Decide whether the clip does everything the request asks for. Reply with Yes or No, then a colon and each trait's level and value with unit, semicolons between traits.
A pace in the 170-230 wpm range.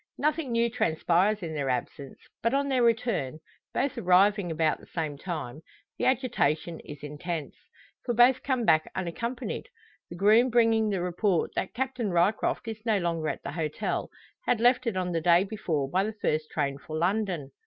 Yes: average, 175 wpm